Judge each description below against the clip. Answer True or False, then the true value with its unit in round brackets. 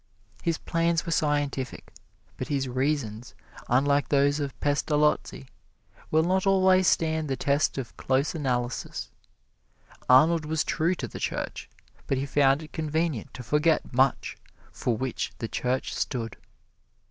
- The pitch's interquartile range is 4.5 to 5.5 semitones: False (3.3 semitones)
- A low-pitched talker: False (145 Hz)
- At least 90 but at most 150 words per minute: True (135 wpm)